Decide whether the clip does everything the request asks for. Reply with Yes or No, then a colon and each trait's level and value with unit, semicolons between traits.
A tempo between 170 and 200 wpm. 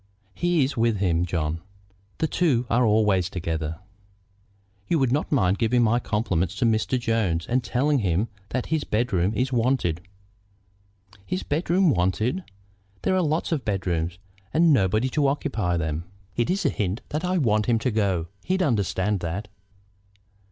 No: average, 155 wpm